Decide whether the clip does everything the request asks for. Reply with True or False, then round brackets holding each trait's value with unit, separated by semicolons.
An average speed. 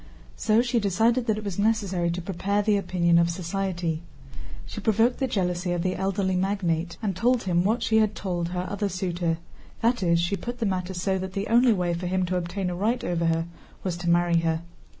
False (215 wpm)